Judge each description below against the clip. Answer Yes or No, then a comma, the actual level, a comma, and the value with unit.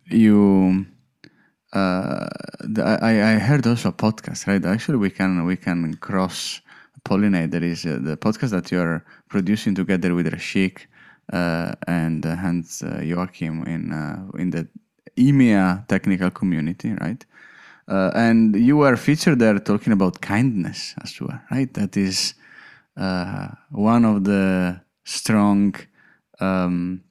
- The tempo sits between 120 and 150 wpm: Yes, average, 140 wpm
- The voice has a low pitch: Yes, very low, 95 Hz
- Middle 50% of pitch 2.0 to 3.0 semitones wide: No, average, 3.4 semitones